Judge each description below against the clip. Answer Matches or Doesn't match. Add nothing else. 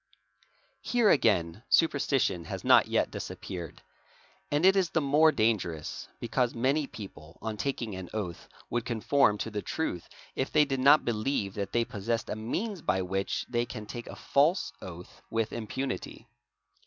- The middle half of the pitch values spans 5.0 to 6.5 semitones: Matches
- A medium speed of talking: Matches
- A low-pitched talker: Matches